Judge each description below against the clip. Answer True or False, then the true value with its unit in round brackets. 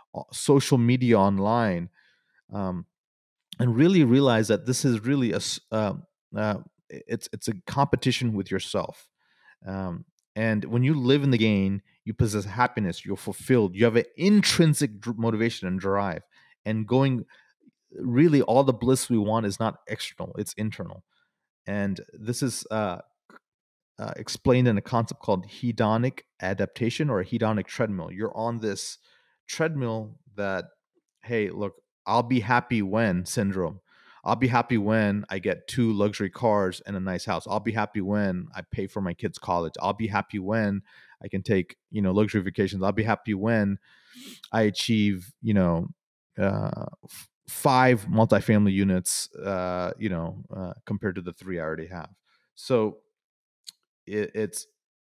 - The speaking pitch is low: True (110 Hz)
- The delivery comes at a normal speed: True (155 wpm)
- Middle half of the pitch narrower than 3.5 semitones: False (3.8 semitones)